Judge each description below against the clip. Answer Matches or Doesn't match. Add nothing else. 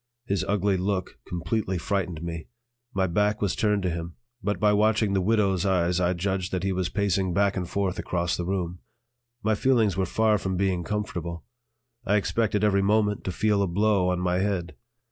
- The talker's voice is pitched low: Matches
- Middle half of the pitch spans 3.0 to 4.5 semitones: Doesn't match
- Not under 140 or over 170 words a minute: Doesn't match